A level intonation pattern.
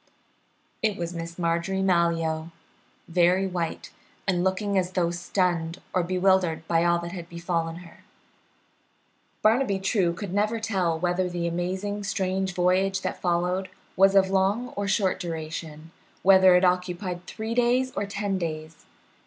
Yes: narrow, 2.2 semitones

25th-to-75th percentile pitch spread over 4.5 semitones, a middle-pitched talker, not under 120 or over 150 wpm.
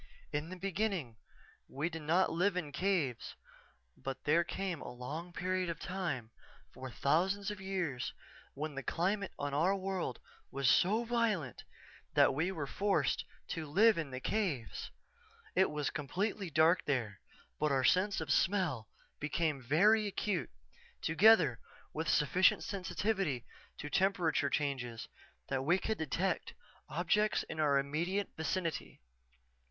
Yes: average, 5.2 semitones; medium, 165 Hz; slow, 135 wpm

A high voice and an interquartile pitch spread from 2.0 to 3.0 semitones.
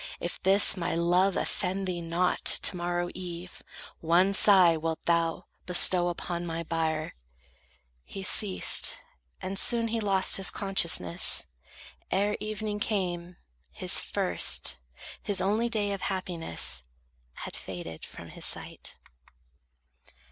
No: medium, 180 Hz; average, 2.7 semitones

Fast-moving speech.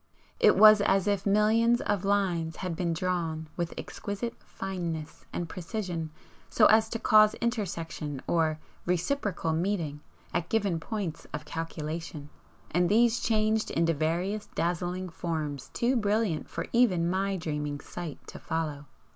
No: average, 140 wpm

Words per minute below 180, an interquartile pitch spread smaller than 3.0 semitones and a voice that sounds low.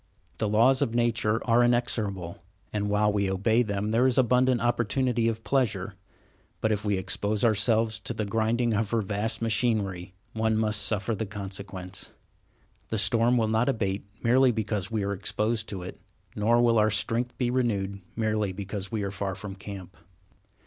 Yes: average, 170 wpm; narrow, 2.6 semitones; low, 110 Hz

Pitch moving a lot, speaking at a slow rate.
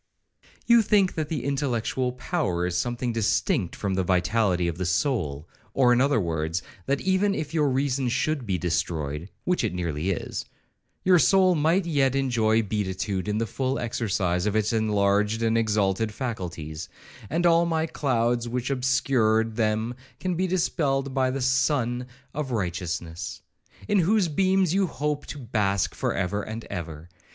No: wide, 6.8 semitones; average, 160 wpm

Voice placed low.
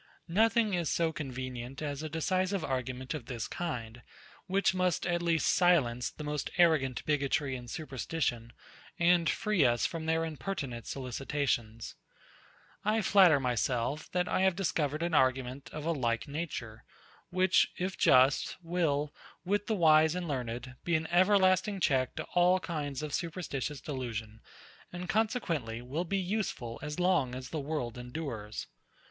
No: medium, 150 Hz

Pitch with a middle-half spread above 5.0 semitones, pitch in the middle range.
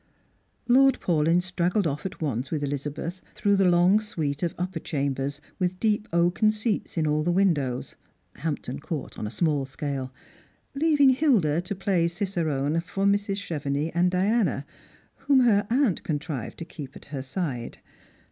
Yes: wide, 5.4 semitones; medium, 170 Hz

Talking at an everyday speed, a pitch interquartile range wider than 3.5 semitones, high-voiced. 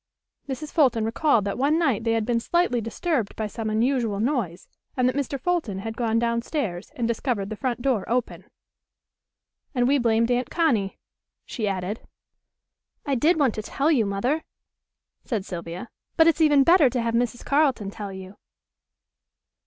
Yes: average, 170 wpm; average, 4.4 semitones; high, 235 Hz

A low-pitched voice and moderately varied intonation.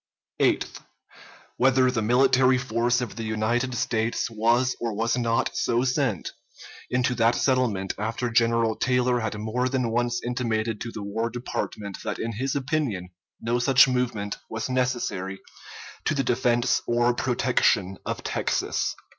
No: low, 120 Hz; narrow, 2.1 semitones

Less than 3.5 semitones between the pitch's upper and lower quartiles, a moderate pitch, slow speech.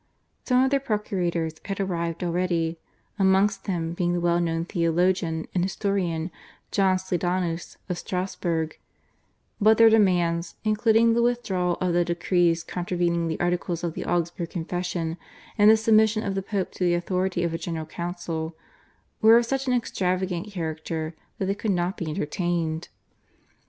No: narrow, 2.6 semitones; medium, 175 Hz; average, 155 wpm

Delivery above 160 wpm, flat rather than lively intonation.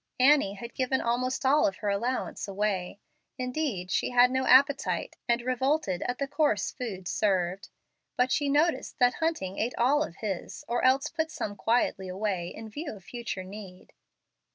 No: average, 170 wpm; average, 5.1 semitones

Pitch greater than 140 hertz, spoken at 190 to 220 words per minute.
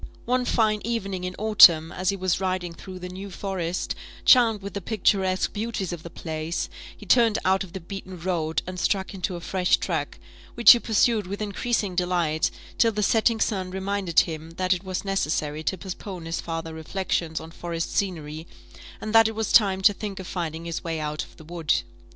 Yes: medium, 185 Hz; average, 200 wpm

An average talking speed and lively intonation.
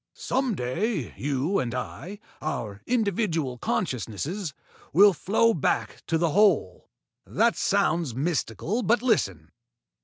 No: slow, 115 wpm; wide, 8.5 semitones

